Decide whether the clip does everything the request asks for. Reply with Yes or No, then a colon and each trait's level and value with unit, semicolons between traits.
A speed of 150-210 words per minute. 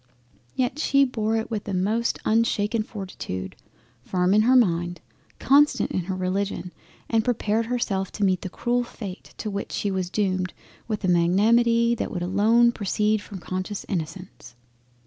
Yes: average, 160 wpm